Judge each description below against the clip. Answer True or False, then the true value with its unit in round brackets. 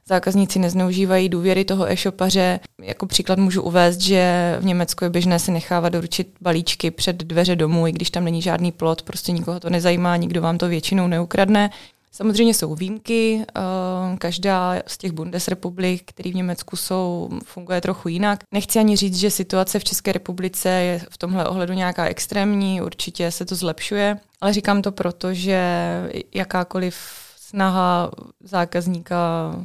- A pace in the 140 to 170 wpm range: True (155 wpm)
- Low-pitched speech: False (185 Hz)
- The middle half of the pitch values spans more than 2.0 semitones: False (1.6 semitones)